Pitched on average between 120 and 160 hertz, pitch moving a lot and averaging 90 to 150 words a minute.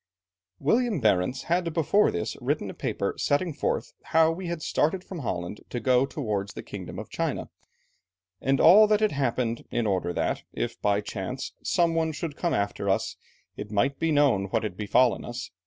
No: low, 135 Hz; wide, 7.9 semitones; average, 185 wpm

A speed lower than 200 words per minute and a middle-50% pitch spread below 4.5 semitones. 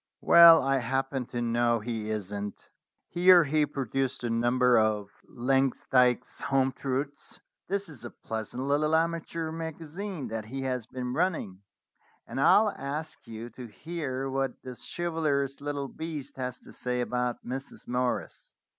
Yes: average, 145 wpm; average, 4.1 semitones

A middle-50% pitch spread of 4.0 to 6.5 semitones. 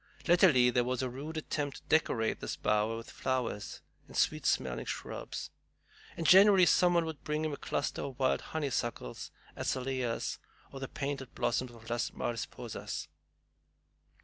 Yes: average, 4.6 semitones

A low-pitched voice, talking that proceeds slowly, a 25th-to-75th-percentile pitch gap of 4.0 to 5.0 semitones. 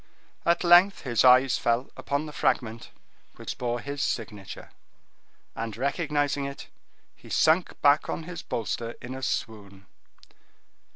Yes: low, 130 Hz; slow, 130 wpm; average, 4.3 semitones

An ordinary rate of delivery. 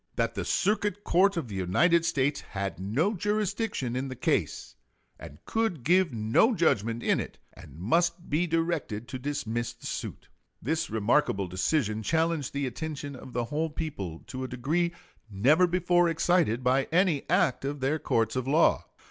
Yes: average, 165 wpm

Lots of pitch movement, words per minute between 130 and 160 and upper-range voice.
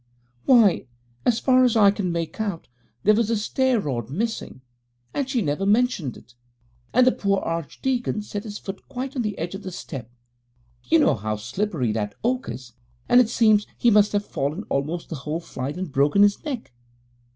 No: wide, 7.6 semitones; average, 190 wpm; high, 205 Hz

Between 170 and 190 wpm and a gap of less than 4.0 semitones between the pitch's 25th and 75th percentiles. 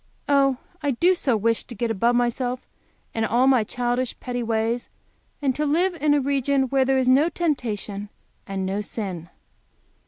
Yes: average, 175 wpm; average, 3.6 semitones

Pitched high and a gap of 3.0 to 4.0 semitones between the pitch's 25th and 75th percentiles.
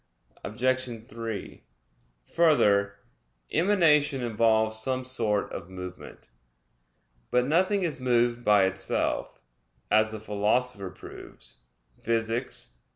No: low, 115 Hz; average, 3.6 semitones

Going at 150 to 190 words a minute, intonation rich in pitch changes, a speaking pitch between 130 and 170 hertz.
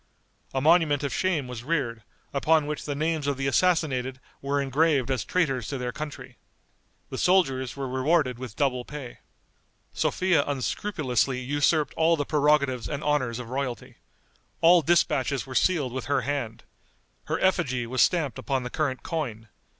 No: average, 160 wpm; average, 3.3 semitones; medium, 140 Hz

